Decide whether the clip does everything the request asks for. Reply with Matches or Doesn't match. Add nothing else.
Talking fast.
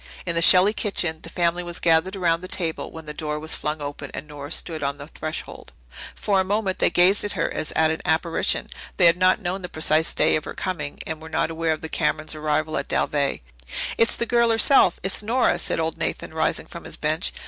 Matches